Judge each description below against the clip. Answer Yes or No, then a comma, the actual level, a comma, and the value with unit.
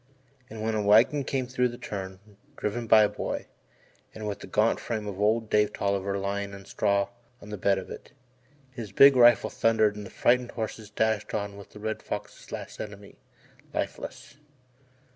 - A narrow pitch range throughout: Yes, narrow, 2.1 semitones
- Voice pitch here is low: Yes, low, 105 Hz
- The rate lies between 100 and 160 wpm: No, average, 180 wpm